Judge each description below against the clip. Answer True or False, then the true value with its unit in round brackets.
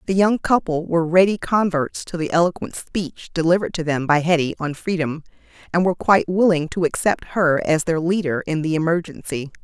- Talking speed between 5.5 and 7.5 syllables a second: True (5.6 syllables/s)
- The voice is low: False (170 Hz)